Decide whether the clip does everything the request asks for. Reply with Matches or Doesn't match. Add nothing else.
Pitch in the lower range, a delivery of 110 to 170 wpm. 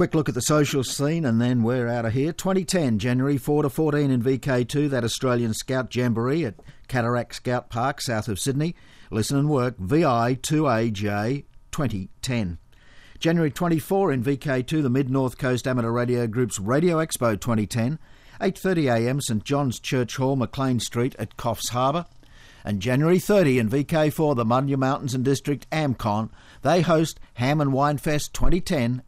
Matches